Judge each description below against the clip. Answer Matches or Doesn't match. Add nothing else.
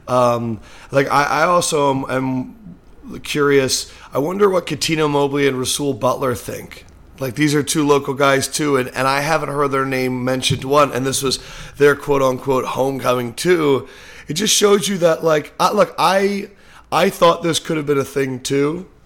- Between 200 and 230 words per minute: Doesn't match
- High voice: Doesn't match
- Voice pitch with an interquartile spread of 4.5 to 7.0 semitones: Doesn't match